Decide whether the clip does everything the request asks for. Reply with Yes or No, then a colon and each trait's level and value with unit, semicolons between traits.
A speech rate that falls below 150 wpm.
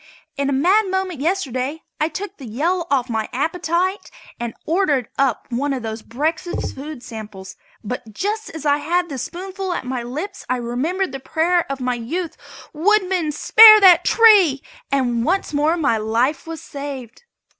No: average, 170 wpm